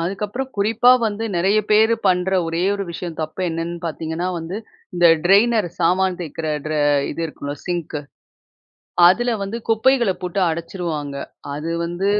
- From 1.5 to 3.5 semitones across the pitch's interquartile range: No, average, 3.9 semitones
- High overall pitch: No, medium, 180 Hz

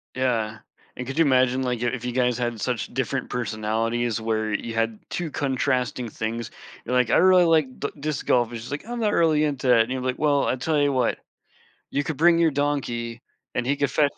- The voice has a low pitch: Yes, low, 125 Hz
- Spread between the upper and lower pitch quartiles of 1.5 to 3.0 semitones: No, average, 3.5 semitones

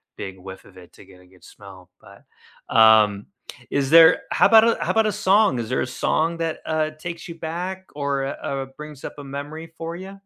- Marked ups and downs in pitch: Yes, wide, 7.5 semitones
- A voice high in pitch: No, medium, 145 Hz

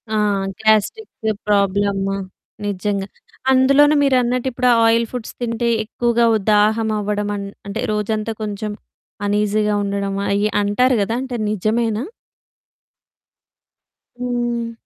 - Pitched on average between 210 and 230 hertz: Yes, high, 215 Hz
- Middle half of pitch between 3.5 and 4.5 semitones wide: No, average, 2.8 semitones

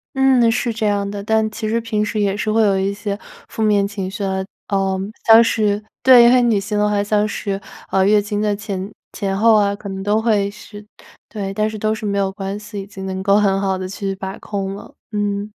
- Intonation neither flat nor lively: No, narrow, 1.5 semitones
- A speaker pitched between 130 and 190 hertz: No, high, 205 Hz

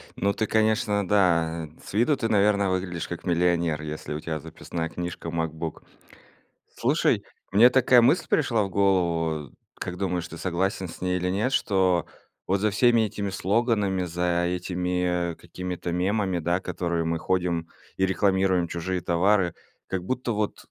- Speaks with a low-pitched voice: Yes, very low, 90 Hz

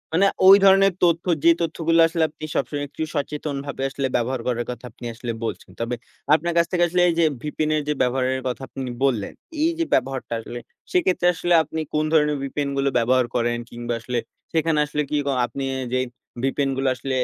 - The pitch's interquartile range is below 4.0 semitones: No, average, 4.4 semitones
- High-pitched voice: No, medium, 140 Hz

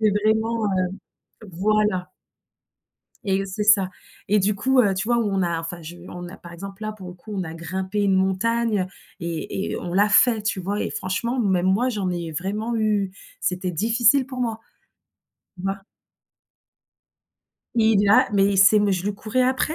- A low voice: No, high, 200 Hz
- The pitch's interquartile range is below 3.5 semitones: Yes, average, 2.9 semitones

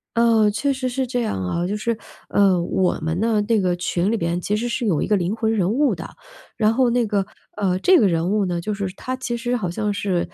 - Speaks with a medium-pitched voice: No, high, 210 Hz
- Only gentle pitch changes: No, average, 4.4 semitones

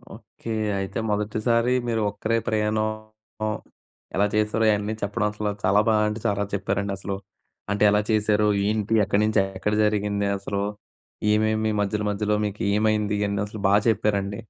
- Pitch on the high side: No, low, 105 Hz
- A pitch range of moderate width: No, narrow, 1.0 semitones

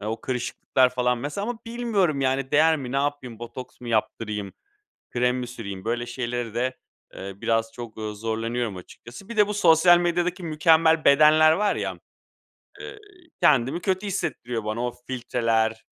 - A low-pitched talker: Yes, low, 125 Hz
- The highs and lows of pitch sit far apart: Yes, wide, 5.9 semitones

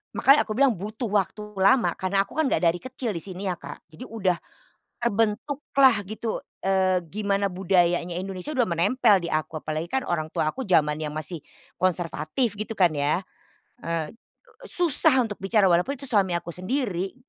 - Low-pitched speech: No, high, 195 Hz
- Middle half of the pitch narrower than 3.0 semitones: No, average, 5.0 semitones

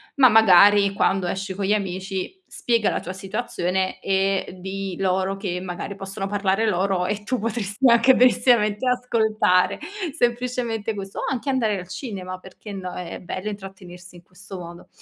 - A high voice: Yes, high, 195 Hz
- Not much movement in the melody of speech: No, average, 3.0 semitones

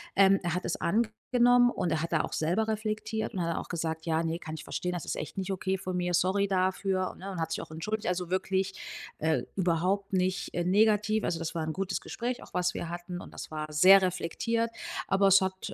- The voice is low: No, medium, 185 Hz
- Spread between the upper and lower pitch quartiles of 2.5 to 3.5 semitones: Yes, average, 2.8 semitones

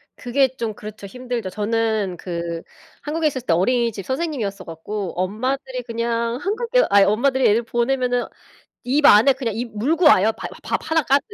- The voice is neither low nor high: No, high, 235 Hz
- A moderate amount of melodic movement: Yes, average, 4.3 semitones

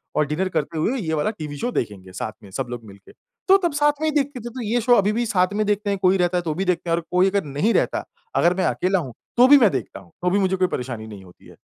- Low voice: No, medium, 185 Hz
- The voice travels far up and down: Yes, wide, 6.6 semitones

